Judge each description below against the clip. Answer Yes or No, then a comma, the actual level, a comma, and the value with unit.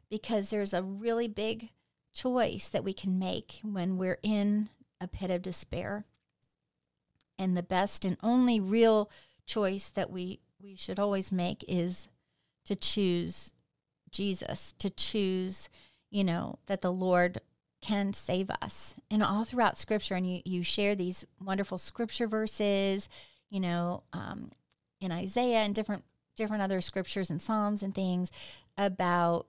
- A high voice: Yes, high, 195 Hz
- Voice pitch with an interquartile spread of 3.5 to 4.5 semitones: No, average, 2.7 semitones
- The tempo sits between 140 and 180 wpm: Yes, average, 145 wpm